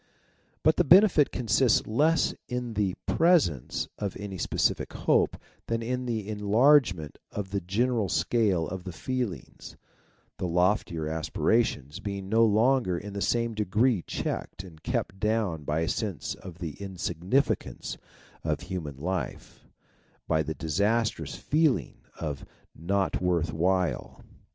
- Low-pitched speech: Yes, low, 100 Hz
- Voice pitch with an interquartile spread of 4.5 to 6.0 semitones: Yes, average, 5.1 semitones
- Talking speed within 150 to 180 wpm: No, slow, 135 wpm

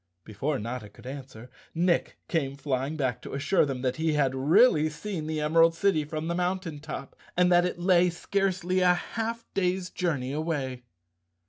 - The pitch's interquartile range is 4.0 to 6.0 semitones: Yes, average, 4.6 semitones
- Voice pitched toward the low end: No, medium, 160 Hz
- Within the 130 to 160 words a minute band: No, average, 170 wpm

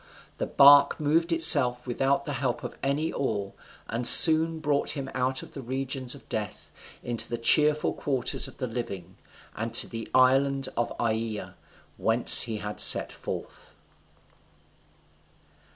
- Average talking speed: Yes, average, 150 wpm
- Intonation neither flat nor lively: Yes, average, 3.3 semitones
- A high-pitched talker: No, low, 130 Hz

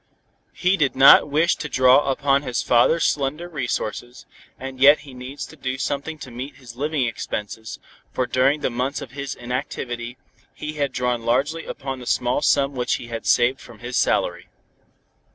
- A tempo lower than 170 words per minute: No, average, 175 wpm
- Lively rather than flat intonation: No, narrow, 2.6 semitones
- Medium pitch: No, low, 130 Hz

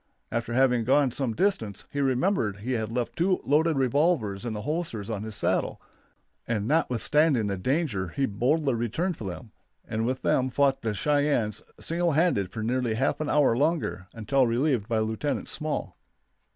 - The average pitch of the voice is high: No, low, 125 Hz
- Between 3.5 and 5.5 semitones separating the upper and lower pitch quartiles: Yes, average, 5.2 semitones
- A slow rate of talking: No, average, 170 wpm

